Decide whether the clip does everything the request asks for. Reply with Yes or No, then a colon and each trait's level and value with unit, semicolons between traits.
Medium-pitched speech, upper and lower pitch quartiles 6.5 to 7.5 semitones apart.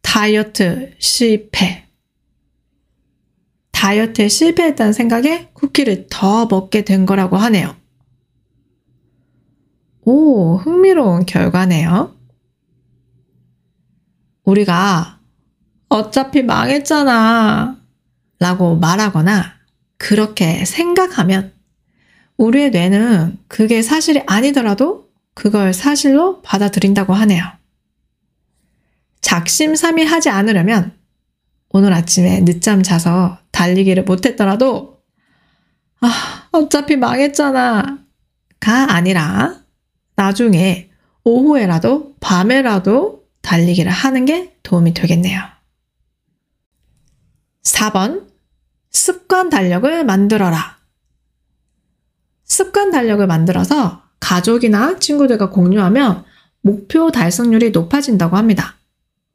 No: high, 200 Hz; wide, 6.8 semitones